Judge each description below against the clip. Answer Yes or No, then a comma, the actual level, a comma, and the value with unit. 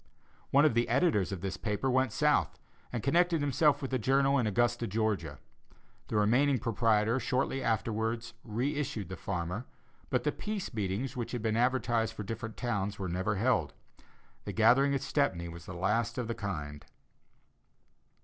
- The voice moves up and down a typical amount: Yes, average, 4.2 semitones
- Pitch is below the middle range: Yes, low, 115 Hz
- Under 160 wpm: No, average, 170 wpm